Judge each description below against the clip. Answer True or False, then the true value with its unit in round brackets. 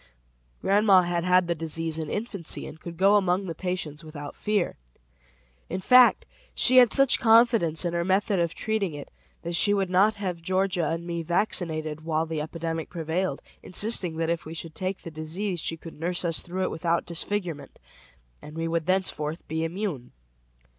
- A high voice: False (170 Hz)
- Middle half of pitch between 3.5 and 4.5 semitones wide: False (3.0 semitones)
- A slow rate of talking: False (180 wpm)